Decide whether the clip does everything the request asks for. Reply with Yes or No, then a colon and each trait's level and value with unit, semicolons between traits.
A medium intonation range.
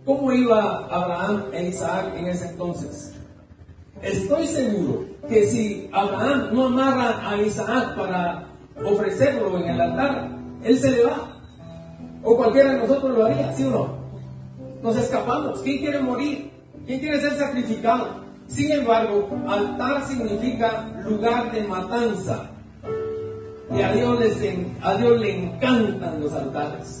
No: wide, 5.9 semitones